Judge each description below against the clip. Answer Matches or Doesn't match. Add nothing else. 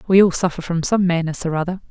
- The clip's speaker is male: Doesn't match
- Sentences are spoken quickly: Matches